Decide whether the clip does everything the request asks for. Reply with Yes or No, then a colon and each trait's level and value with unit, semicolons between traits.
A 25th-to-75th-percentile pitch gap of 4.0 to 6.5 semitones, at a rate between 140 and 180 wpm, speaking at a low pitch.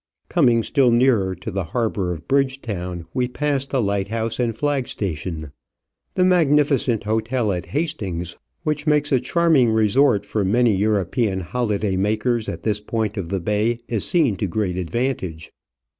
Yes: average, 5.2 semitones; average, 160 wpm; low, 110 Hz